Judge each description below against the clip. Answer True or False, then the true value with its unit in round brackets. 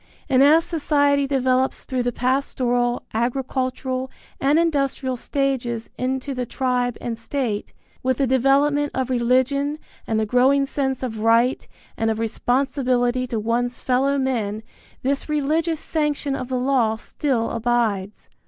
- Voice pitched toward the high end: True (255 Hz)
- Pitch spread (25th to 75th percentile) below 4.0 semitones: True (2.4 semitones)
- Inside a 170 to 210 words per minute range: False (135 wpm)